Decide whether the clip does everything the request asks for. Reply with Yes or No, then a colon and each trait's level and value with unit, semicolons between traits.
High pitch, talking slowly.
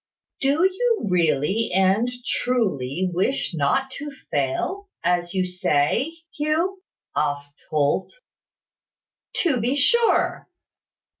Yes: high, 210 Hz; slow, 95 wpm